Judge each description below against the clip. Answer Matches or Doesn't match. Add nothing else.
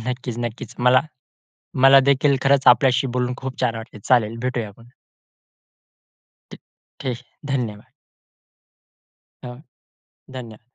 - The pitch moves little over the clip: Matches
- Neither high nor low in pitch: Doesn't match